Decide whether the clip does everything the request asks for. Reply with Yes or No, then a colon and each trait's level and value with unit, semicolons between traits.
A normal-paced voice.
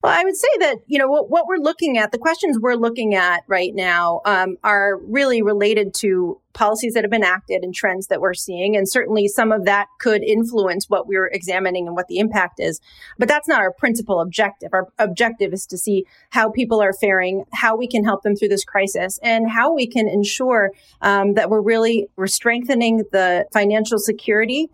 No: fast, 210 wpm